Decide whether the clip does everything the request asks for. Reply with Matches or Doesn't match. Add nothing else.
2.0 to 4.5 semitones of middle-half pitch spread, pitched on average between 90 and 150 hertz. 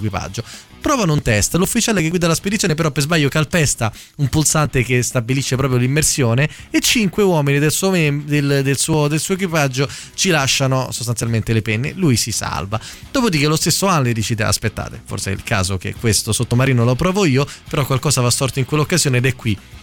Doesn't match